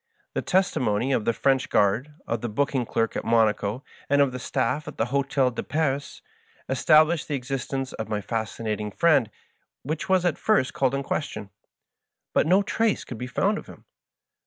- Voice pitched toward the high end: No, low, 130 Hz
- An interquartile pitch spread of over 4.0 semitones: Yes, average, 4.4 semitones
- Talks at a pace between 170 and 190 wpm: Yes, average, 185 wpm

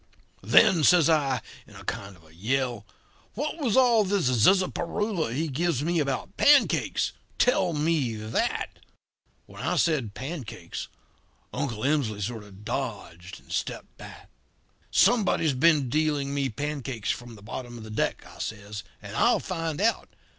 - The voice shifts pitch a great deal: Yes, wide, 7.2 semitones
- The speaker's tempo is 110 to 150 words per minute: Yes, average, 145 wpm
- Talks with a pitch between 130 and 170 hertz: Yes, medium, 140 Hz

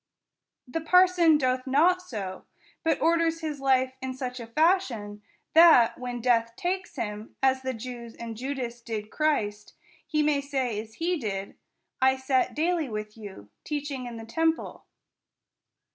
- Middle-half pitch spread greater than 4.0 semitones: Yes, wide, 5.4 semitones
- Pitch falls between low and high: No, very high, 260 Hz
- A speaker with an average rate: Yes, average, 150 wpm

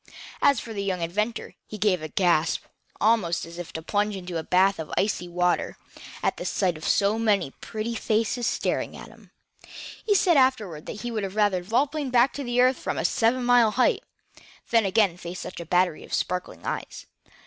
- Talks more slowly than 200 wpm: No, fast, 205 wpm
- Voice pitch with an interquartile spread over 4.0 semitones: Yes, average, 5.0 semitones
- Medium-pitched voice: No, high, 205 Hz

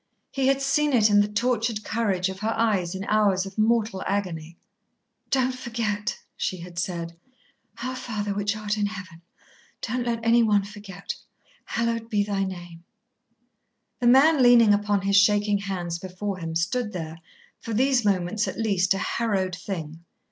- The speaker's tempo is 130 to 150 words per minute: No, average, 160 wpm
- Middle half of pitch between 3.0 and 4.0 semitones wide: Yes, average, 3.5 semitones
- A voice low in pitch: No, high, 205 Hz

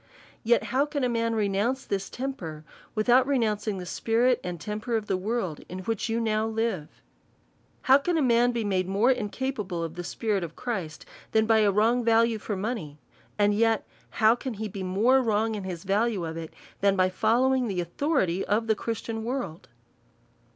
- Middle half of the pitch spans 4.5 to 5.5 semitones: No, average, 3.8 semitones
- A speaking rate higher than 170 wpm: Yes, average, 185 wpm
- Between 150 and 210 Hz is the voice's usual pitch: No, high, 220 Hz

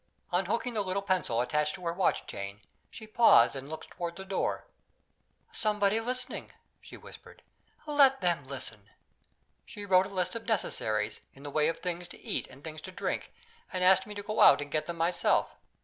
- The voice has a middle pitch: Yes, medium, 180 Hz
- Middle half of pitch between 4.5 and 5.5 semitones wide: Yes, average, 5.2 semitones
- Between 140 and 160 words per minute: No, average, 190 wpm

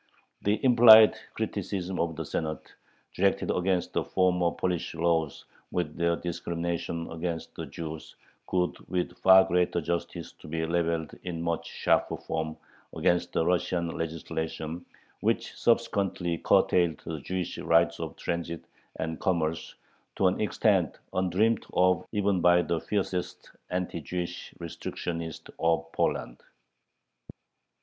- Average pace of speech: No, slow, 125 wpm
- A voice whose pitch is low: Yes, very low, 85 Hz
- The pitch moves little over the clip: Yes, narrow, 1.9 semitones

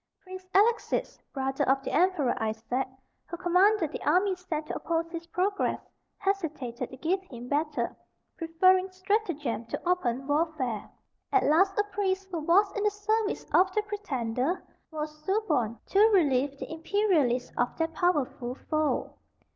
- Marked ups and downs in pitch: Yes, wide, 5.8 semitones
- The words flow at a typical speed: Yes, average, 145 wpm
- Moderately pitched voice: No, very high, 330 Hz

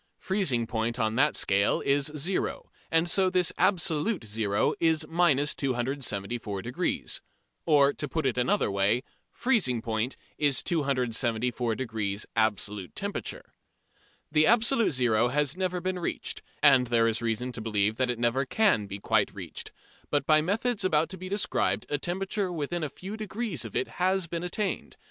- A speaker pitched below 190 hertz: Yes, medium, 140 Hz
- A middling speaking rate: Yes, average, 155 wpm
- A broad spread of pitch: Yes, wide, 7.4 semitones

